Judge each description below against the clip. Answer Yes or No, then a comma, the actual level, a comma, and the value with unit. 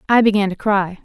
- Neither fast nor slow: No, fast, 230 wpm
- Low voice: No, high, 200 Hz